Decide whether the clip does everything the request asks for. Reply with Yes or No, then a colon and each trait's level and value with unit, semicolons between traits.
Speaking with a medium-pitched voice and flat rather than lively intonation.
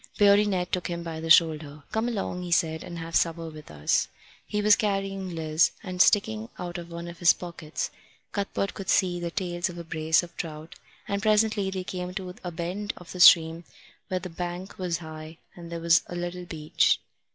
Yes: medium, 175 Hz; narrow, 2.3 semitones